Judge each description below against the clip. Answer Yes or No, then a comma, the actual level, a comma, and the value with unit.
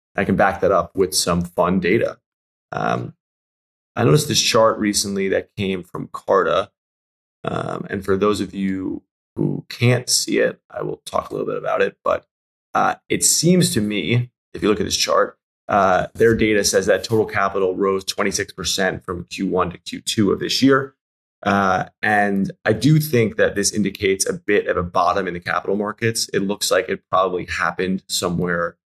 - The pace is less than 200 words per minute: Yes, average, 185 wpm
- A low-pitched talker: Yes, low, 100 Hz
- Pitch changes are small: No, average, 3.0 semitones